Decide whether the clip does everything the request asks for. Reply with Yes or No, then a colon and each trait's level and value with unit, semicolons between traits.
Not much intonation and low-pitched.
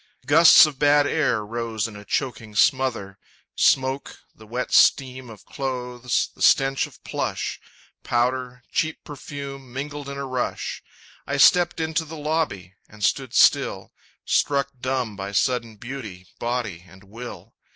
No: average, 3.7 semitones; low, 125 Hz